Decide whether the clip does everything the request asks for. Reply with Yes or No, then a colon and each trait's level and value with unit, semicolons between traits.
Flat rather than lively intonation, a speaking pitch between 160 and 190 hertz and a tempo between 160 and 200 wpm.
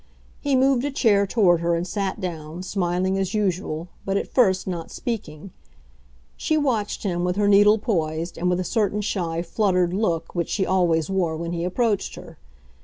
No: average, 3.3 semitones; medium, 185 Hz; average, 180 wpm